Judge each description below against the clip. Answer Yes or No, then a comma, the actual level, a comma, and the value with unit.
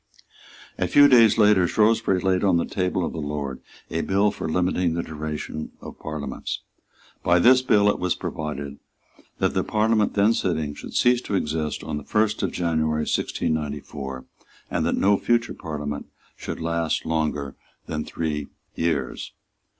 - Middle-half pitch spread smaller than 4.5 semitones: No, average, 5.0 semitones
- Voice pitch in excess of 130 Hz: No, very low, 85 Hz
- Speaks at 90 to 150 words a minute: No, average, 160 wpm